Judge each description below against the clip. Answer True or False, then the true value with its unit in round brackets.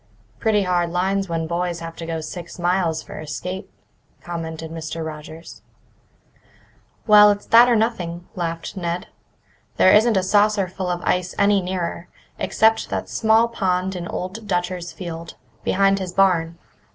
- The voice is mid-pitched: True (180 Hz)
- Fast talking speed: False (150 wpm)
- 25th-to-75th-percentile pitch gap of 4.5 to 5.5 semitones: False (2.8 semitones)